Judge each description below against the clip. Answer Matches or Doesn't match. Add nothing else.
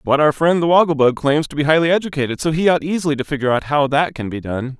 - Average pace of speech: Doesn't match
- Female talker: Doesn't match